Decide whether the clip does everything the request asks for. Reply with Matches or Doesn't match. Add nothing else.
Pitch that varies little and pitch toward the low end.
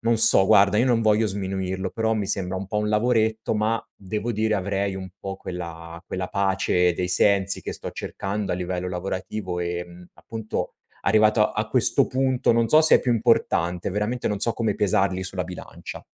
Doesn't match